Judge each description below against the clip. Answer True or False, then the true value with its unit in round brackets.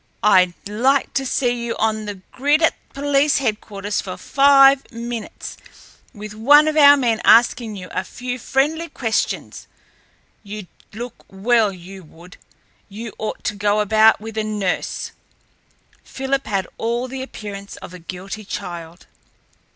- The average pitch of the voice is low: False (220 Hz)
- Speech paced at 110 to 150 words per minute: True (145 wpm)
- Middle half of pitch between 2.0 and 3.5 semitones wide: False (4.7 semitones)